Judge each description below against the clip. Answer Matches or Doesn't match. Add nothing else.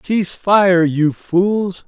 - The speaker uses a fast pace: Doesn't match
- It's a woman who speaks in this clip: Doesn't match